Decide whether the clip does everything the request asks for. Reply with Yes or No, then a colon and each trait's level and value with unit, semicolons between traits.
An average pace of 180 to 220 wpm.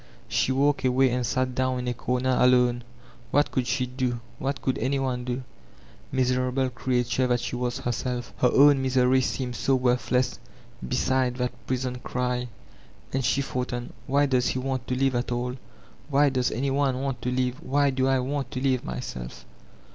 Yes: average, 185 wpm